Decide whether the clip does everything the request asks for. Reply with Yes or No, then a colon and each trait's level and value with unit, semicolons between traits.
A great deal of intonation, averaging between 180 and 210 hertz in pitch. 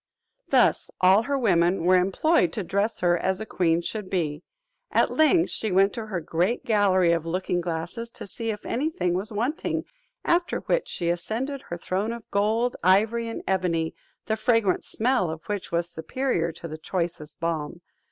No: average, 4.8 semitones; high, 190 Hz